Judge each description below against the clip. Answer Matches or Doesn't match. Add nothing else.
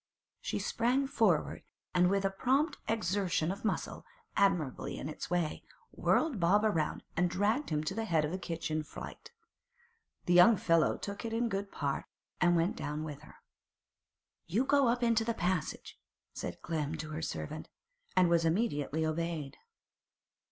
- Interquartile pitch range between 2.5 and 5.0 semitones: Doesn't match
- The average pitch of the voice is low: Doesn't match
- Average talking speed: Matches